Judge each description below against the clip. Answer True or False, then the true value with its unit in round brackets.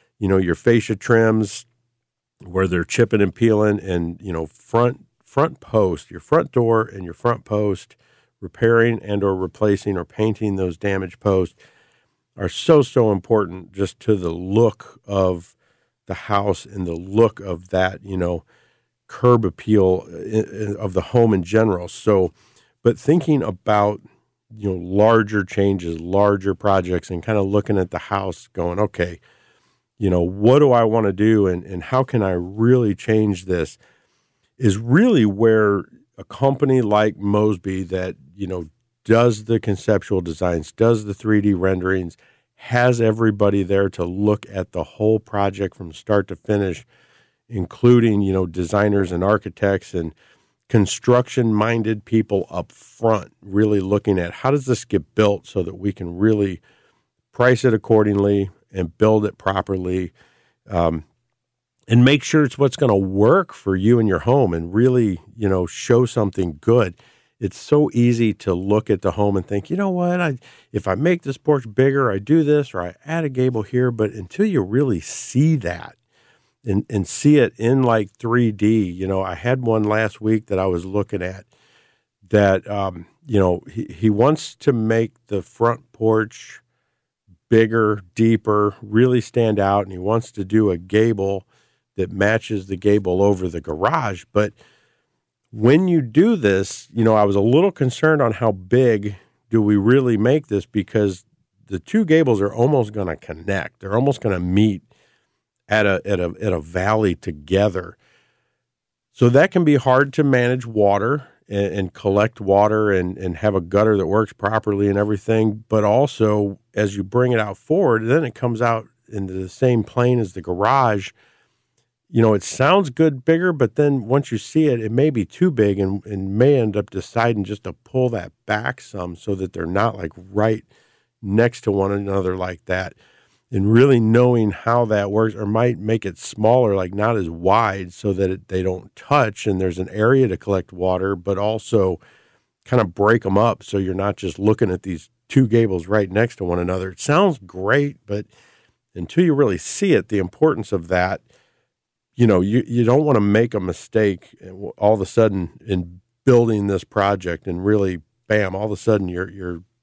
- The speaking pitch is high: False (105 Hz)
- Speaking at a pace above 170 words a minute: True (180 wpm)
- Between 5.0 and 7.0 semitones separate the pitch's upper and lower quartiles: False (3.7 semitones)